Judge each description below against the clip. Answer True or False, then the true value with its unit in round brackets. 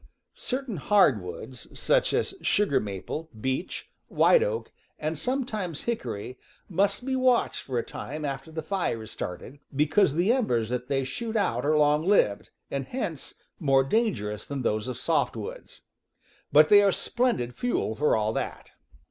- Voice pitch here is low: False (150 Hz)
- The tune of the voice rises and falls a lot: True (8.8 semitones)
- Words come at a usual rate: True (155 wpm)